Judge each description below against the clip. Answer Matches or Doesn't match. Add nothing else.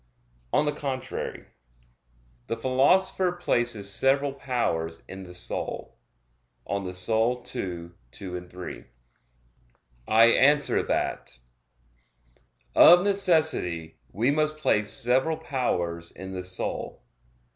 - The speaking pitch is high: Doesn't match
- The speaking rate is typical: Doesn't match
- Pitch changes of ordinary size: Doesn't match